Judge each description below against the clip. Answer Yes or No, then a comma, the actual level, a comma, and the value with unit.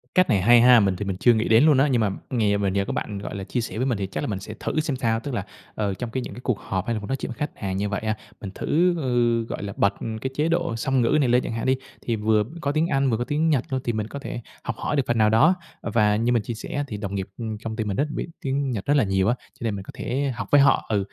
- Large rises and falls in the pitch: No, average, 4.4 semitones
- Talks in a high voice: No, low, 115 Hz